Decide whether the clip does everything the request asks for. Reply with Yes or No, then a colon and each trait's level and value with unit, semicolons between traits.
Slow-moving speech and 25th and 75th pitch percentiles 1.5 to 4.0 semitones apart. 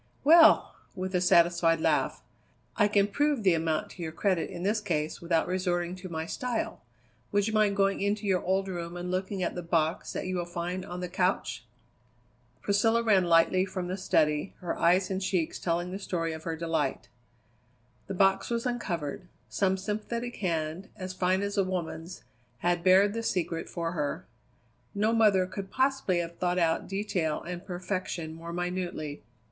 No: average, 175 wpm; average, 2.8 semitones